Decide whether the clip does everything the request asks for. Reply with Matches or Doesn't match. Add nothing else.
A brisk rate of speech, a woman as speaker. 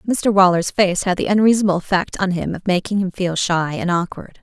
Matches